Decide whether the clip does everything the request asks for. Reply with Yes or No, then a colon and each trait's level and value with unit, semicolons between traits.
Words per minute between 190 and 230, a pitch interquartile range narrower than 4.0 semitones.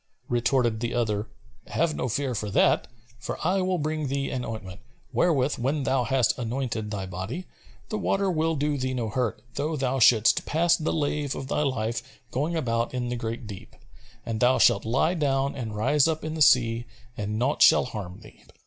No: average, 195 wpm; average, 4.5 semitones